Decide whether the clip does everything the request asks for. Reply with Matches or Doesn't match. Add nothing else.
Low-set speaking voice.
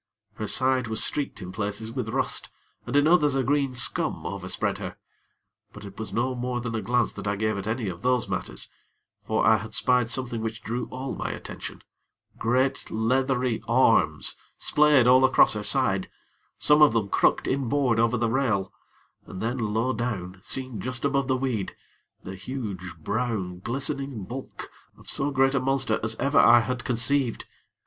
Matches